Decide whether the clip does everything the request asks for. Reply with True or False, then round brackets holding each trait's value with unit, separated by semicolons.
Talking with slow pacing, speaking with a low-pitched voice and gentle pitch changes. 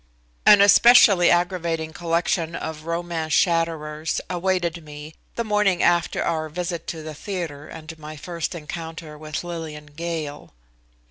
False (130 wpm; 165 Hz; 2.0 semitones)